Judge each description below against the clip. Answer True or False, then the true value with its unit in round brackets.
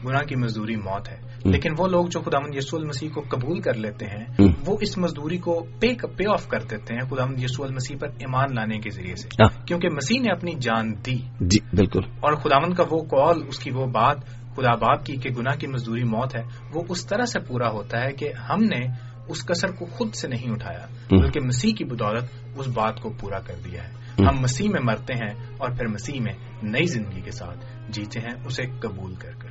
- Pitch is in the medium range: False (125 Hz)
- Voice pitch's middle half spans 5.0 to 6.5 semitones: False (3.7 semitones)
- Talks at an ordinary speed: False (235 wpm)